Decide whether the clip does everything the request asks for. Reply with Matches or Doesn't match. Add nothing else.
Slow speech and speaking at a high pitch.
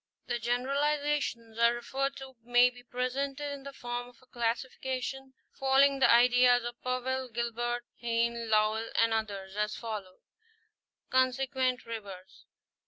Matches